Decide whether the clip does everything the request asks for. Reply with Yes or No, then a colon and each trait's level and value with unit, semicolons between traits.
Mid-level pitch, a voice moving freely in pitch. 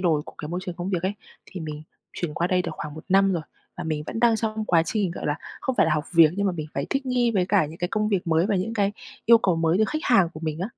No: medium, 180 Hz; average, 4.4 semitones